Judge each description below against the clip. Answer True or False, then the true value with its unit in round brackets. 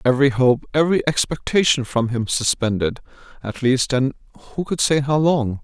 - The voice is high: False (135 Hz)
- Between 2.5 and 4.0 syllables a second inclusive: False (5.2 syllables/s)